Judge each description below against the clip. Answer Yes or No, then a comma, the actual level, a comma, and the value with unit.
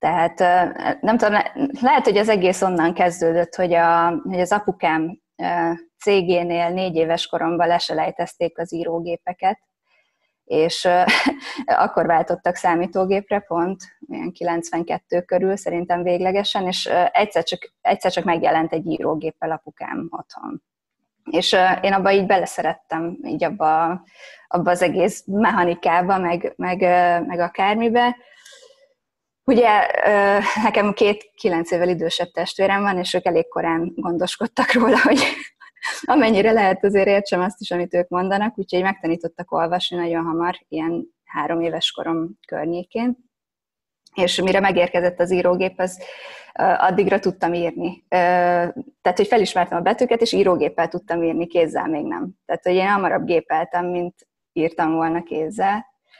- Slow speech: No, average, 130 wpm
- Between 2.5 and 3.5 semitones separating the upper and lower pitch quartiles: Yes, average, 2.8 semitones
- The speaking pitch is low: No, medium, 180 Hz